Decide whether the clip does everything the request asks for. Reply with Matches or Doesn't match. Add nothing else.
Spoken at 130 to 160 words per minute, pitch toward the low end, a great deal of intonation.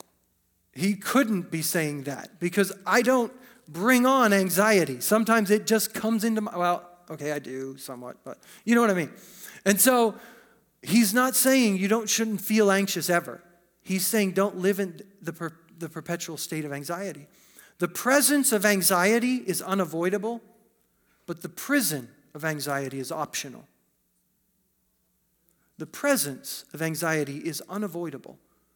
Doesn't match